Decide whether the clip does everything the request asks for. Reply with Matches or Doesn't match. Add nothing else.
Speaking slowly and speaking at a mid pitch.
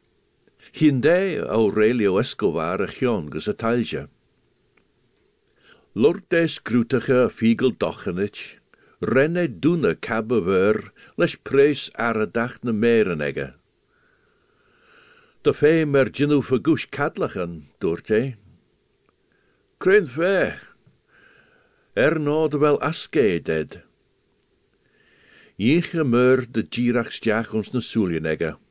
Matches